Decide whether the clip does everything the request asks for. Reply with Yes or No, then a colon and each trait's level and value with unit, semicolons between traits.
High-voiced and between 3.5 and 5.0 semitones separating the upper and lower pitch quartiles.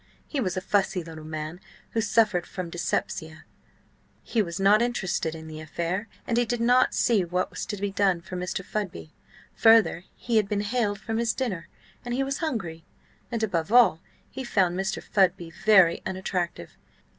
Yes: high, 195 Hz; average, 4.7 semitones